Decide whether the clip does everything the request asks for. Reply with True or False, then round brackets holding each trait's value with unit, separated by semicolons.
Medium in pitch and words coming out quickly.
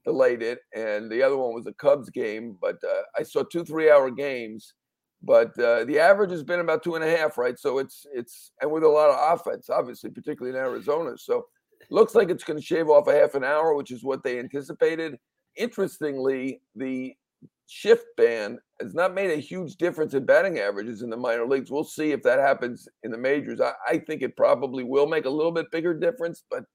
True (165 Hz; 220 wpm)